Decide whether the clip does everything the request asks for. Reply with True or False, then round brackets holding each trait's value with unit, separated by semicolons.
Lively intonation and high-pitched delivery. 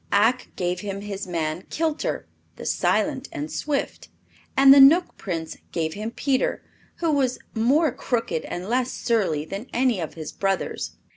True (7.1 semitones; 225 Hz)